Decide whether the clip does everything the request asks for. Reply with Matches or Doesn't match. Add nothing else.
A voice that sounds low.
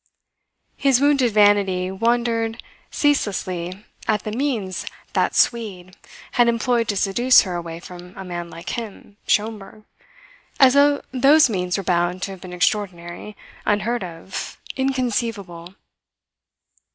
Doesn't match